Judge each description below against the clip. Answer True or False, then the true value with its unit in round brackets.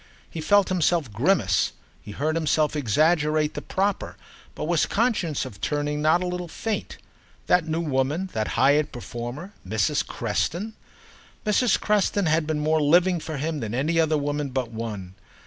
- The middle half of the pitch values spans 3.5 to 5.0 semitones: True (4.6 semitones)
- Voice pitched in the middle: True (155 Hz)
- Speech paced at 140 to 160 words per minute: True (155 wpm)